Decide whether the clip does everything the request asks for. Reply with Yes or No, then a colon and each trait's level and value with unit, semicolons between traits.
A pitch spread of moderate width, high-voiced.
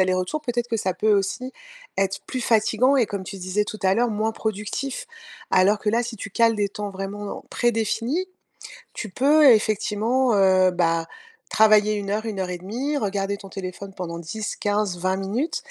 Yes: average, 3.1 semitones; high, 210 Hz